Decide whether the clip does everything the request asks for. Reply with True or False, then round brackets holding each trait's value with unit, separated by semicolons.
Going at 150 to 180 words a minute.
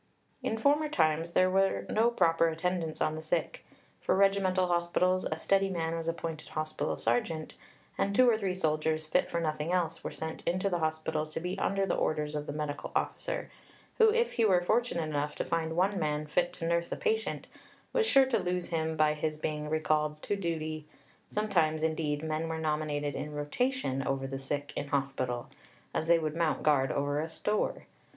False (190 wpm)